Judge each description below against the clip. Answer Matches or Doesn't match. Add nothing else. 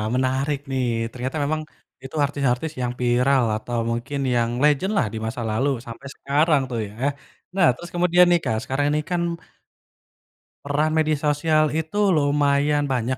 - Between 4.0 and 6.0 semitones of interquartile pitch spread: Doesn't match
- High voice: Doesn't match